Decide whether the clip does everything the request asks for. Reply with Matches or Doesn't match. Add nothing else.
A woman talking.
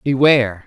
Doesn't match